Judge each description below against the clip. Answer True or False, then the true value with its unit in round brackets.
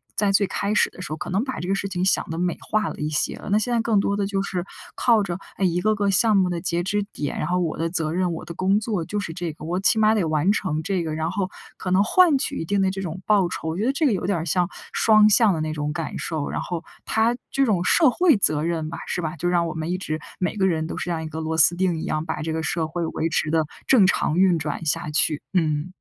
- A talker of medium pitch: True (180 Hz)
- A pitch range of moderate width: True (3.8 semitones)